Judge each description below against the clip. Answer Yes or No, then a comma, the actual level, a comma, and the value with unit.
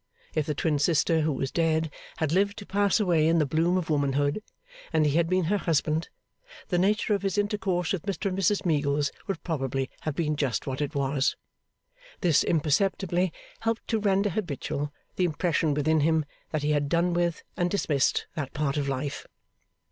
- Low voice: No, medium, 160 Hz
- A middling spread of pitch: Yes, average, 4.1 semitones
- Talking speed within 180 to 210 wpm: Yes, average, 185 wpm